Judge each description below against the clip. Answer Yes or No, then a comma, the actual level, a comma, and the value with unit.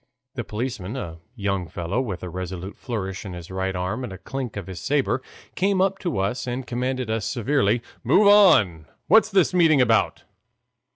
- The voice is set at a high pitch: No, low, 115 Hz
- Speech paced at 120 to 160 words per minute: No, average, 180 wpm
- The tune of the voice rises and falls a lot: Yes, wide, 6.0 semitones